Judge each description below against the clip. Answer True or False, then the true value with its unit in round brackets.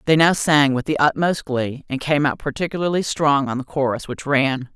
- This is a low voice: False (145 Hz)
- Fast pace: True (215 wpm)